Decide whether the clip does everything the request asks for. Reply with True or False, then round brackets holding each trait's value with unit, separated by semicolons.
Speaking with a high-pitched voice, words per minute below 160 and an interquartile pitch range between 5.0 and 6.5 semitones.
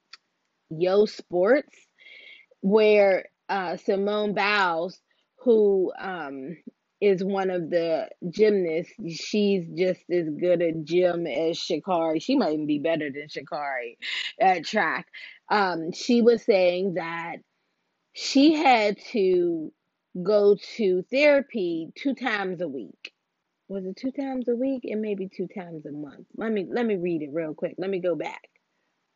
True (195 Hz; 140 wpm; 5.3 semitones)